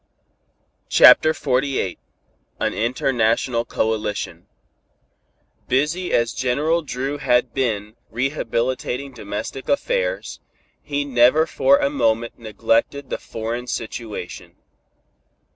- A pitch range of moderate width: Yes, average, 3.8 semitones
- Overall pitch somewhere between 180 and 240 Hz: No, low, 125 Hz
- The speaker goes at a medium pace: No, slow, 90 wpm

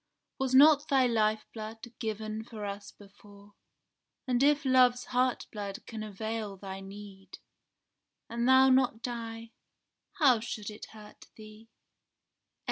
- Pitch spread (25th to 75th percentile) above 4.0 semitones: No, average, 3.2 semitones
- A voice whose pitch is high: Yes, high, 225 Hz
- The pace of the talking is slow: Yes, slow, 120 wpm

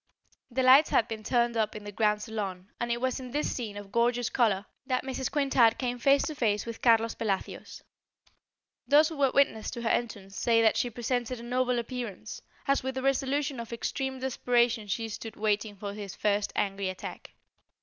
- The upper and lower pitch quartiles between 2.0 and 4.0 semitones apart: Yes, average, 3.3 semitones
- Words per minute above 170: Yes, average, 195 wpm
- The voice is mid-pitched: No, high, 235 Hz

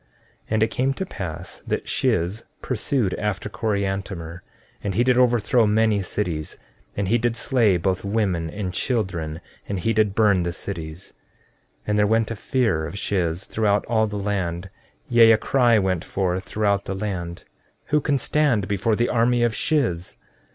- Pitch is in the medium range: No, low, 105 Hz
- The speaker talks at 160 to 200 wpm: Yes, average, 165 wpm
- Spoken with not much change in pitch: No, average, 3.6 semitones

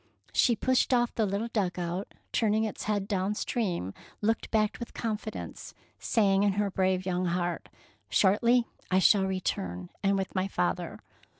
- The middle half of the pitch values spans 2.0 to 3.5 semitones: Yes, average, 2.8 semitones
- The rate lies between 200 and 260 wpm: No, average, 180 wpm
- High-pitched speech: Yes, high, 195 Hz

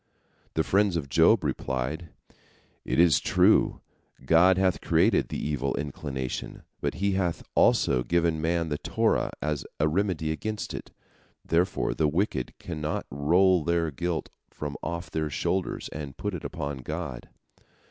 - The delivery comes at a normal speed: Yes, average, 145 wpm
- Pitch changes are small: No, average, 3.3 semitones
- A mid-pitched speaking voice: No, very low, 80 Hz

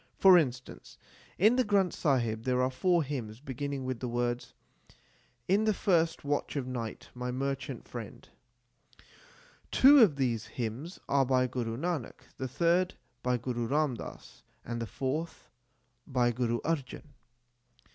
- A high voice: No, low, 130 Hz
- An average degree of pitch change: Yes, average, 5.0 semitones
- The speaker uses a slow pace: No, average, 145 wpm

